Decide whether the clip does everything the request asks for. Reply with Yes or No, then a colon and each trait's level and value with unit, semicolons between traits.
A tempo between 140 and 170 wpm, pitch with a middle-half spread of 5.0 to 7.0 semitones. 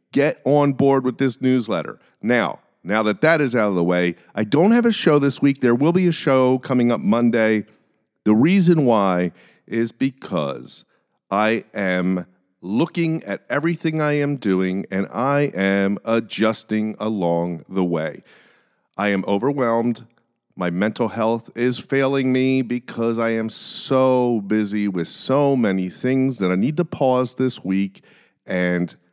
Yes: average, 155 wpm; wide, 5.5 semitones